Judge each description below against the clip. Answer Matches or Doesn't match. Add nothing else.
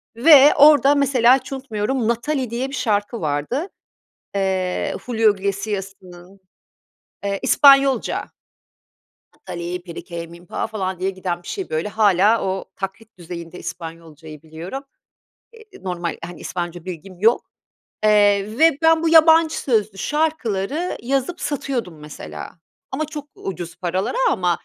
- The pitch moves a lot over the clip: Matches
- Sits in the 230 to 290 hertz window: Doesn't match